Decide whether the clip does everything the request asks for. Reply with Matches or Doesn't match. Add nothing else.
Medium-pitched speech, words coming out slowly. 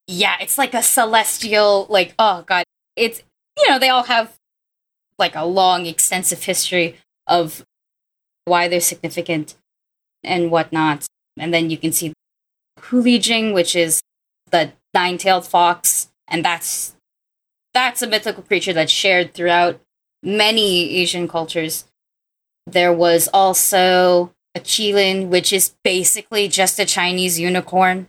Matches